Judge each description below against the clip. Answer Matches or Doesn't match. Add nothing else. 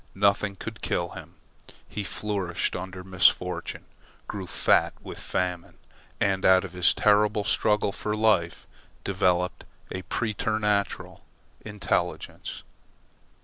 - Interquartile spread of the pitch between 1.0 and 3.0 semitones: Matches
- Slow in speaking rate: Matches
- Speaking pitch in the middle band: Doesn't match